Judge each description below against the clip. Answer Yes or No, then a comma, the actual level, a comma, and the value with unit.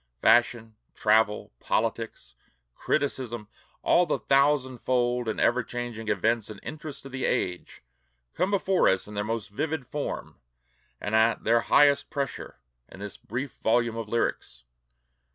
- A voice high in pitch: No, low, 120 Hz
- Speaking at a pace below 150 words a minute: Yes, slow, 135 wpm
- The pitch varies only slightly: No, average, 3.7 semitones